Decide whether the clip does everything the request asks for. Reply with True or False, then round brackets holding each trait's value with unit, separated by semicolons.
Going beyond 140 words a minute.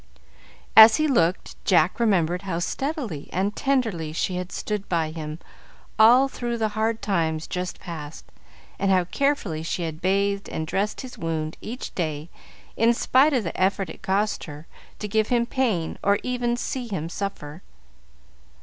True (160 wpm)